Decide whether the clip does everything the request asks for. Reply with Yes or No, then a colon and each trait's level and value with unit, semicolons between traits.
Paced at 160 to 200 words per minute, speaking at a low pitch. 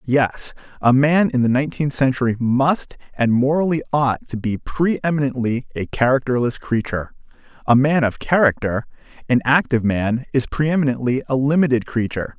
No: average, 150 wpm; low, 130 Hz